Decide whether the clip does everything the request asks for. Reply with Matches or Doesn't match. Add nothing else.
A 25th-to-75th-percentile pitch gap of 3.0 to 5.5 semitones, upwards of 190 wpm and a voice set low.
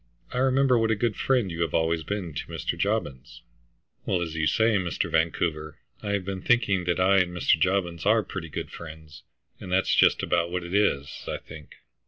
Matches